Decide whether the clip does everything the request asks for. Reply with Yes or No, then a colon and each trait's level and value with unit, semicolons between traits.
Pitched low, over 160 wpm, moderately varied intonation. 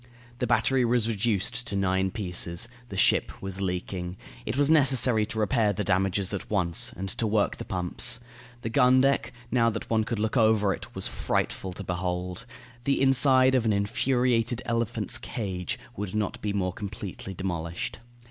Yes: low, 105 Hz; average, 170 wpm; average, 4.1 semitones